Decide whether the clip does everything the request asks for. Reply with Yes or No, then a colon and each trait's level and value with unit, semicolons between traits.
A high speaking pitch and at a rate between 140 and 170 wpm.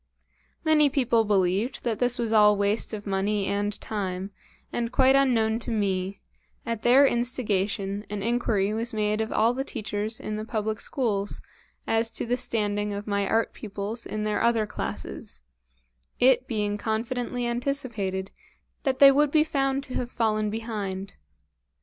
Yes: high, 220 Hz; average, 155 wpm